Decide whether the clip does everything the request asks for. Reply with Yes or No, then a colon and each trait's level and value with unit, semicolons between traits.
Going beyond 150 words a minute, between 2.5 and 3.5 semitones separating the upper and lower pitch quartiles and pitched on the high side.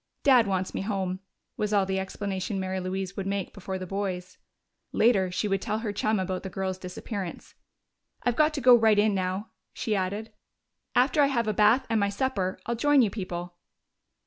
Yes: average, 195 wpm; average, 2.8 semitones; high, 200 Hz